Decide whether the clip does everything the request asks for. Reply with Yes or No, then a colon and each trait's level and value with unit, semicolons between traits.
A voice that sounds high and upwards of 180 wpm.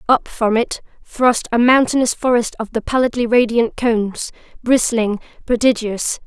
No: high, 235 Hz; slow, 135 wpm